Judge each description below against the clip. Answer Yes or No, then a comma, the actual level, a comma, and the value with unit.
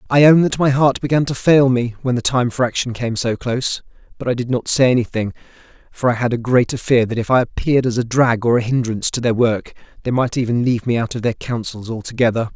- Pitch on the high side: No, low, 120 Hz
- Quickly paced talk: Yes, fast, 250 wpm